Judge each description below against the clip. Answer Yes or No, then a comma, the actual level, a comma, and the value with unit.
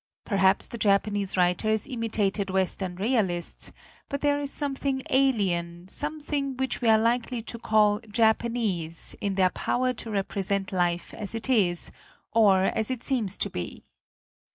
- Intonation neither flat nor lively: Yes, average, 4.4 semitones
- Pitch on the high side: Yes, high, 215 Hz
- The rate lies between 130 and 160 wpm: Yes, average, 145 wpm